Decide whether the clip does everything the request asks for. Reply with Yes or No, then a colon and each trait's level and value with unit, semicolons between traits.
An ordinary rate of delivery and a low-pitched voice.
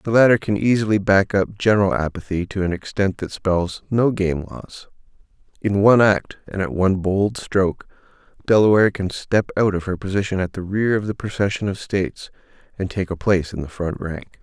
Yes: average, 195 wpm; low, 100 Hz